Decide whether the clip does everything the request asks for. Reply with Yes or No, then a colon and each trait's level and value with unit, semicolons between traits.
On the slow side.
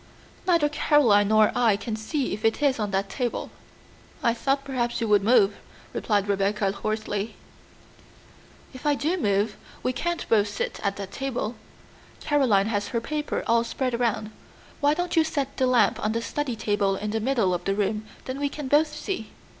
No: average, 185 wpm